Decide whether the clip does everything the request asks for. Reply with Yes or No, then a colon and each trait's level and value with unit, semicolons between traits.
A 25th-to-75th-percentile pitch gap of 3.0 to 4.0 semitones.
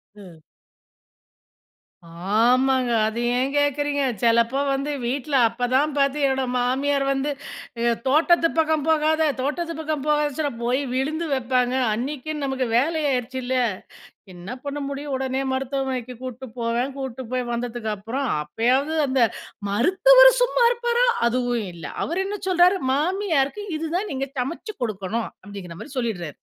Yes: average, 3.7 semitones